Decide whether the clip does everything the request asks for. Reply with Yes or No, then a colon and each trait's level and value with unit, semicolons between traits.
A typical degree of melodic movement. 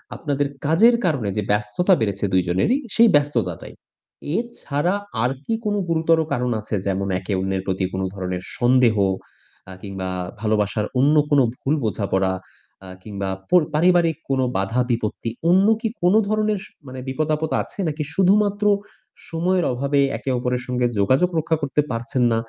No: wide, 8.1 semitones